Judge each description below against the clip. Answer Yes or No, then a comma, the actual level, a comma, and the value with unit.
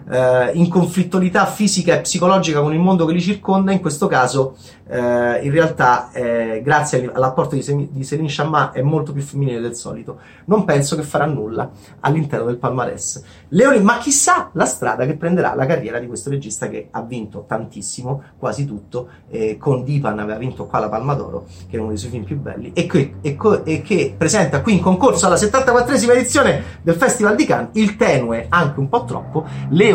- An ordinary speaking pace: No, fast, 195 wpm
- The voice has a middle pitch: Yes, medium, 145 Hz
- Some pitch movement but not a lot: No, wide, 6.4 semitones